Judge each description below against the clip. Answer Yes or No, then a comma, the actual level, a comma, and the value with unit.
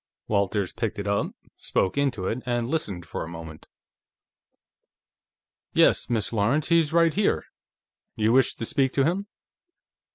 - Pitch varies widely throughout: Yes, wide, 6.0 semitones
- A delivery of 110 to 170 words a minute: Yes, average, 140 wpm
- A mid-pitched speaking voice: No, low, 115 Hz